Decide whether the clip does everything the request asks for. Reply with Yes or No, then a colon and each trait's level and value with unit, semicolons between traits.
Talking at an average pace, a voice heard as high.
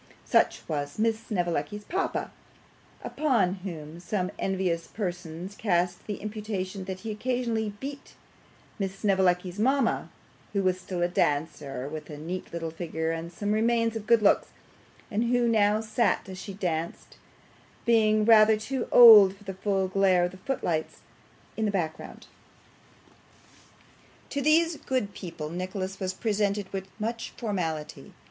Yes: average, 145 wpm; high, 195 Hz